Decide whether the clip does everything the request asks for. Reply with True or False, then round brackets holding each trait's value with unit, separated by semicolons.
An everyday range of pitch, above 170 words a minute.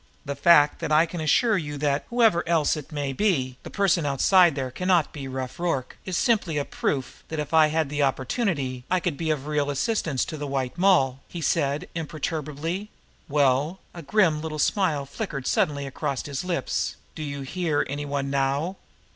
True (3.7 semitones; 190 wpm)